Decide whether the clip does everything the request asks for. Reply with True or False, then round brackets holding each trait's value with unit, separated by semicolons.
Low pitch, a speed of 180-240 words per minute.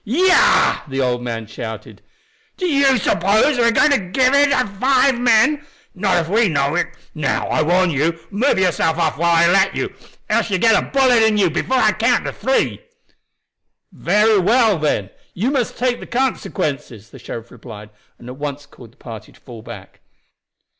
False (195 Hz; 190 wpm)